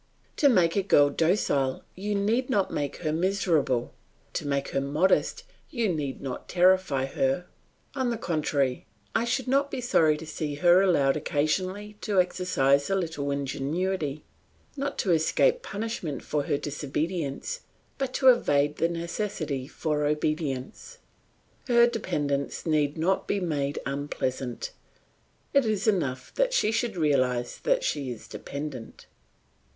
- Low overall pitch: No, medium, 160 Hz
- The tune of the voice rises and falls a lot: Yes, wide, 6.3 semitones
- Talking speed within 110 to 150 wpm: Yes, average, 140 wpm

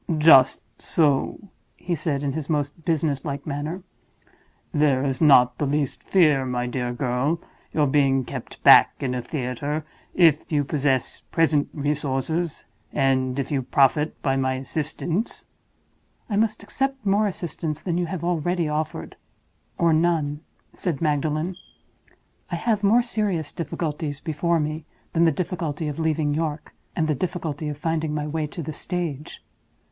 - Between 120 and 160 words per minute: Yes, average, 150 wpm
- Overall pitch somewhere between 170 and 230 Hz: No, medium, 150 Hz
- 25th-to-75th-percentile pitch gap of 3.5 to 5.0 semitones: No, average, 3.1 semitones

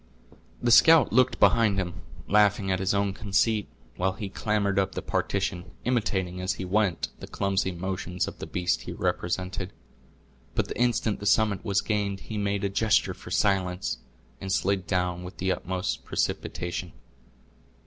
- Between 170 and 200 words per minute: No, average, 160 wpm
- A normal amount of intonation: No, narrow, 2.1 semitones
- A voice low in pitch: Yes, very low, 95 Hz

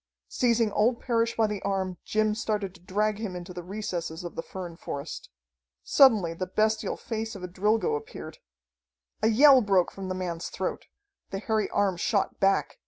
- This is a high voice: Yes, high, 205 Hz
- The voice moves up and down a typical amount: Yes, average, 3.2 semitones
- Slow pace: No, average, 175 wpm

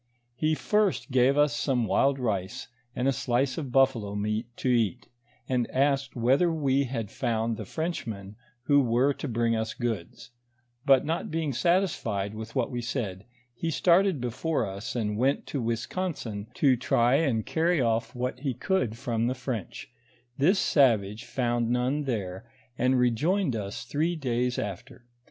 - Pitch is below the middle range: Yes, low, 125 Hz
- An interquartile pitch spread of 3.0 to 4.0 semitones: Yes, average, 3.7 semitones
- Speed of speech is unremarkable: Yes, average, 160 wpm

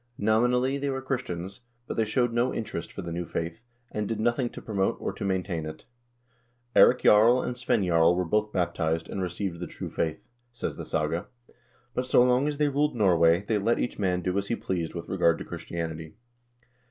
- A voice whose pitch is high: No, low, 100 Hz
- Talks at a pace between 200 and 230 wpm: Yes, fast, 205 wpm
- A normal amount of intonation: No, wide, 6.1 semitones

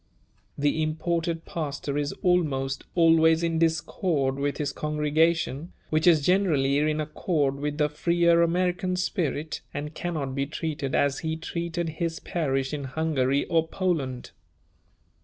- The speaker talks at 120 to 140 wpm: Yes, slow, 135 wpm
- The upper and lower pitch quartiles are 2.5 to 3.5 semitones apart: Yes, average, 2.9 semitones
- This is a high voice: No, medium, 155 Hz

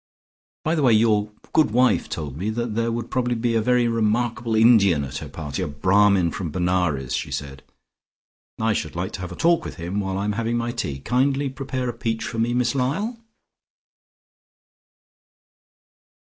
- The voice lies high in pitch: No, low, 110 Hz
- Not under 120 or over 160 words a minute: No, average, 180 wpm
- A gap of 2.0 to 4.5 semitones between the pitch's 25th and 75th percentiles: No, average, 5.0 semitones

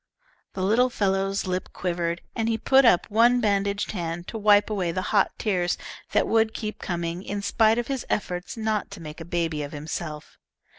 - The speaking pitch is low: No, high, 195 Hz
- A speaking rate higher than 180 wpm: Yes, average, 190 wpm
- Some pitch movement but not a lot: Yes, average, 4.1 semitones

